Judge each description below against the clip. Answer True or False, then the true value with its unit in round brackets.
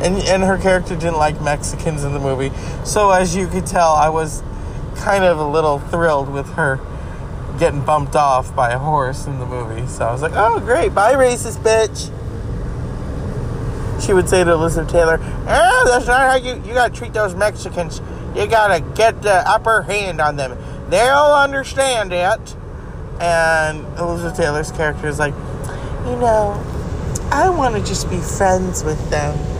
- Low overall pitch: False (165 Hz)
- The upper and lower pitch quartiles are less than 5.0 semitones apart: False (5.4 semitones)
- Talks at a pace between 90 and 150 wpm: False (175 wpm)